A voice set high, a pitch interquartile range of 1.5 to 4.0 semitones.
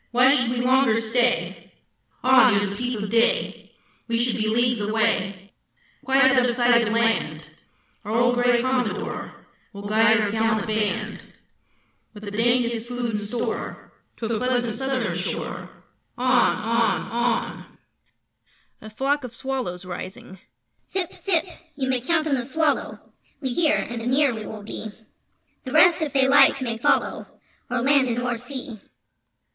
Yes: high, 240 Hz; average, 2.8 semitones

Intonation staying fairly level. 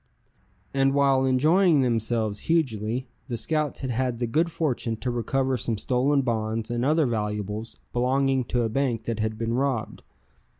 No: average, 3.2 semitones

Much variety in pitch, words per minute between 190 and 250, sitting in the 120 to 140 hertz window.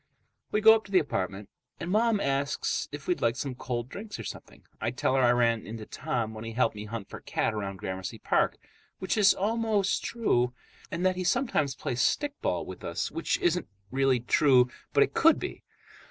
Yes: wide, 8.9 semitones; average, 200 wpm; low, 135 Hz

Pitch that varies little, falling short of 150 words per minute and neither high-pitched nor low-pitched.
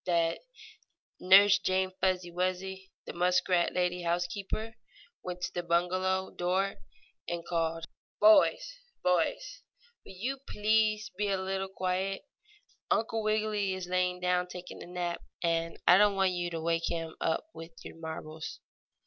Yes: narrow, 2.1 semitones; average, 140 wpm; medium, 180 Hz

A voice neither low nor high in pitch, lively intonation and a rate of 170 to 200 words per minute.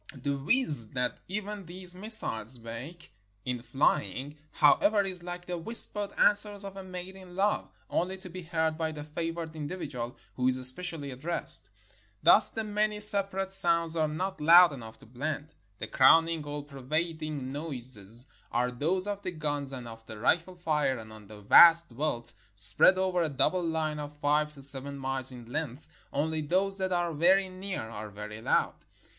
Yes: medium, 155 Hz; wide, 5.7 semitones; average, 175 wpm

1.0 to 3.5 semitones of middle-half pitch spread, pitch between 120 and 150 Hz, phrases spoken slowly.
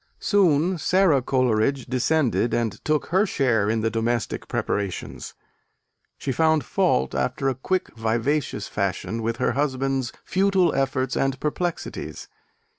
No: average, 5.1 semitones; low, 135 Hz; slow, 125 wpm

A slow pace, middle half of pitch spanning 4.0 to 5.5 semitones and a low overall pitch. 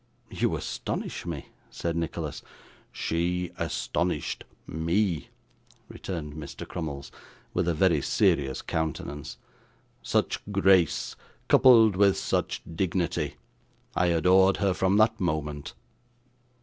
No: slow, 100 wpm; average, 3.4 semitones; very low, 85 Hz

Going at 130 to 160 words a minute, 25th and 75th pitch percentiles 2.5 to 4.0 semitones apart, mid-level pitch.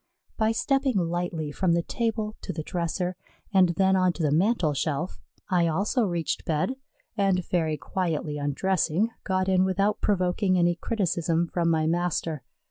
Yes: average, 155 wpm; average, 2.8 semitones; medium, 180 Hz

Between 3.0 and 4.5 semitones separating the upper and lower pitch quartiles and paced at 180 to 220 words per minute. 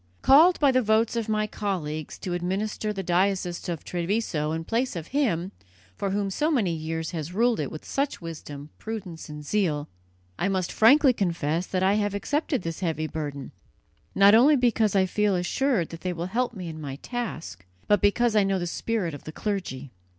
No: average, 5.1 semitones; average, 195 wpm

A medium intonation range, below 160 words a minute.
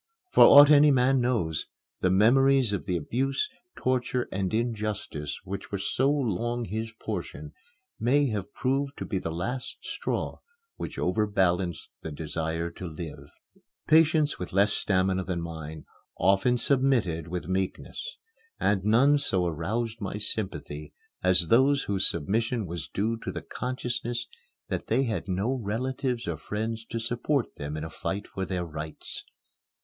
No: wide, 5.7 semitones; average, 150 wpm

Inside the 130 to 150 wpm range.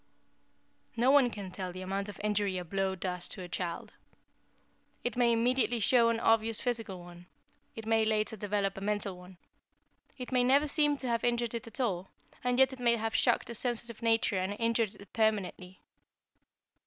No: average, 185 wpm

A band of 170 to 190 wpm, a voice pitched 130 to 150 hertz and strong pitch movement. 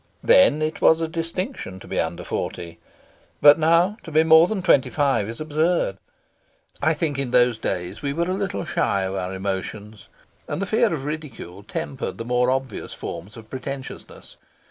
Yes: average, 180 wpm; medium, 140 Hz; wide, 7.1 semitones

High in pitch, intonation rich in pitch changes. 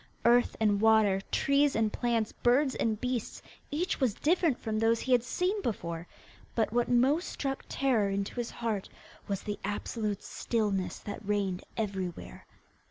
No: high, 225 Hz; average, 3.8 semitones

